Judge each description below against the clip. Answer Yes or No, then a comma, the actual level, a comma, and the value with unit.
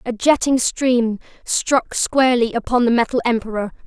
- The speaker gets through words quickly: No, average, 140 wpm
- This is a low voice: No, high, 240 Hz